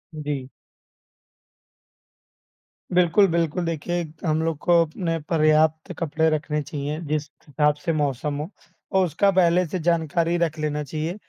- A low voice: No, medium, 160 Hz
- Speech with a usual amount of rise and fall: No, narrow, 2.2 semitones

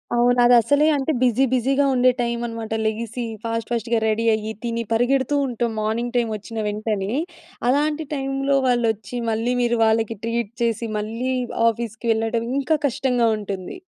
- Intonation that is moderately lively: No, narrow, 2.1 semitones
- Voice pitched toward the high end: Yes, high, 235 Hz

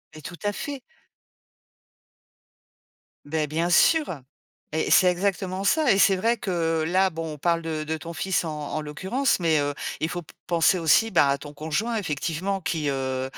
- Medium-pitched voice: Yes, medium, 170 Hz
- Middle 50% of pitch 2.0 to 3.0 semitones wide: No, average, 3.8 semitones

